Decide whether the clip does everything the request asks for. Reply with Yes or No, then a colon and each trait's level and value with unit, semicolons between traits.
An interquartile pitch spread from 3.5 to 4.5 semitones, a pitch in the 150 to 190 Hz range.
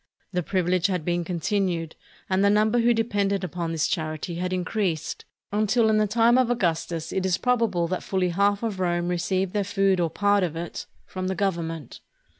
No: average, 2.9 semitones; medium, 185 Hz